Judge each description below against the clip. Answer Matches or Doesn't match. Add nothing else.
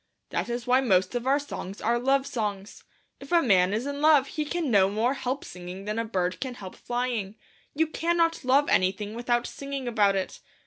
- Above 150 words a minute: Matches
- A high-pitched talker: Matches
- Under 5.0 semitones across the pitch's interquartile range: Doesn't match